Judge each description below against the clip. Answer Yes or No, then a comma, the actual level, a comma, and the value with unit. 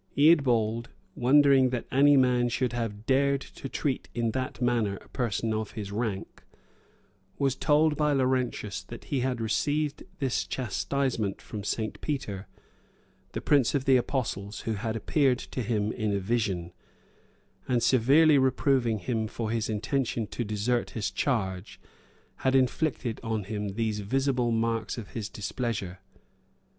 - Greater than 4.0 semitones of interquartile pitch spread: No, average, 3.6 semitones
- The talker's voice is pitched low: Yes, low, 120 Hz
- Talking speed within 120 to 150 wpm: Yes, average, 145 wpm